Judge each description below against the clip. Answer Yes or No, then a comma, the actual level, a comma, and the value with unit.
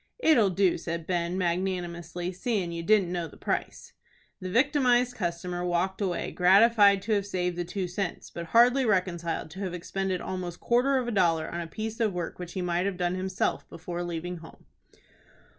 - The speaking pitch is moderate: Yes, medium, 180 Hz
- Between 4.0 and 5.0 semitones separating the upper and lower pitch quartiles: No, average, 2.7 semitones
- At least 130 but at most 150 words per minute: No, average, 185 wpm